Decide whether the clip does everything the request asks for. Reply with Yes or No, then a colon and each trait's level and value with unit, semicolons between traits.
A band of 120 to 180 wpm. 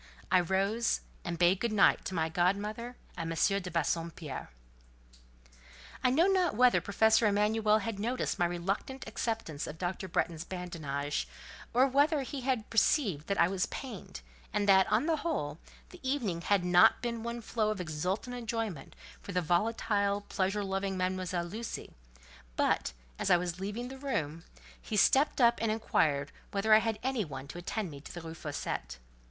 Yes: average, 170 wpm